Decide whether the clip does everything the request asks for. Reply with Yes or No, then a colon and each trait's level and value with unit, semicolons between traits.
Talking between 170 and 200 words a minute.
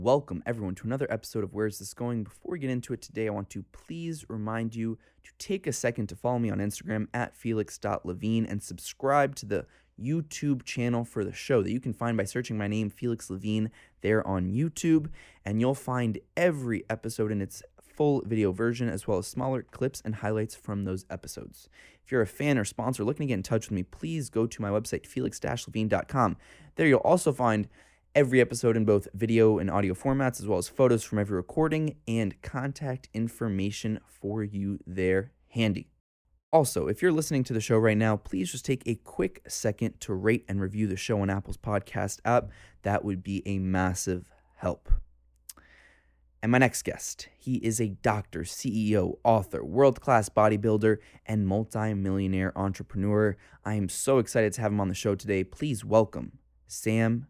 Yes: average, 190 wpm